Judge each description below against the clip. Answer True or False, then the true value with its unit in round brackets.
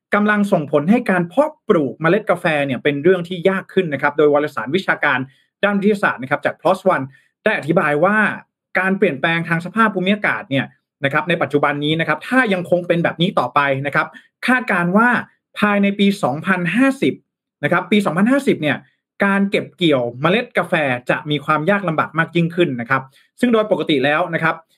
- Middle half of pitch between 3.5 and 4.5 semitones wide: False (5.1 semitones)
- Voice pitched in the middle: True (175 Hz)